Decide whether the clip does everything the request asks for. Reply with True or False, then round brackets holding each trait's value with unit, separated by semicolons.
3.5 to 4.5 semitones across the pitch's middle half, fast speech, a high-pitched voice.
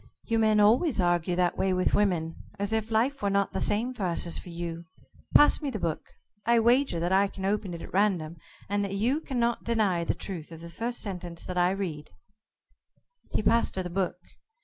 True (4.2 semitones; 210 wpm; 195 Hz)